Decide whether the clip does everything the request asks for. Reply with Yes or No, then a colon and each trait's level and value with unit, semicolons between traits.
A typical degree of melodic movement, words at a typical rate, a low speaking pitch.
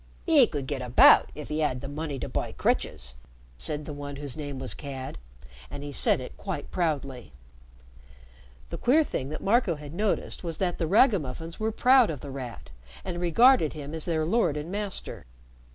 No: average, 5.0 semitones; average, 185 wpm; medium, 155 Hz